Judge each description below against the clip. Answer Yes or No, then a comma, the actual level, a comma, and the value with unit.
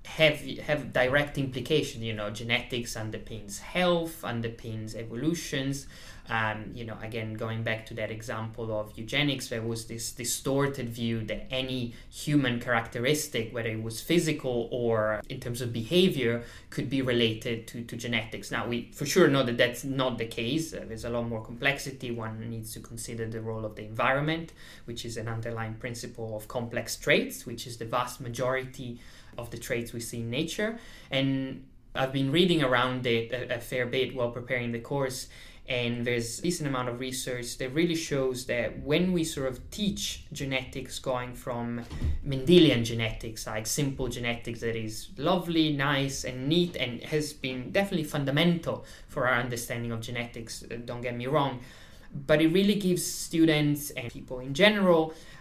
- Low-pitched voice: Yes, low, 125 Hz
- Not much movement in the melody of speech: No, average, 3.3 semitones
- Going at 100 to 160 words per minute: No, average, 170 wpm